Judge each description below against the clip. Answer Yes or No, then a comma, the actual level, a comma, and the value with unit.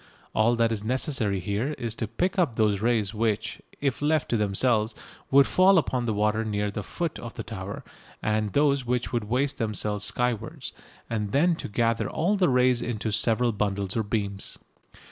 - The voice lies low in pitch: Yes, low, 115 Hz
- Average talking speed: Yes, average, 185 wpm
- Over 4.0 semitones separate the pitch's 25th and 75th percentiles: No, average, 3.4 semitones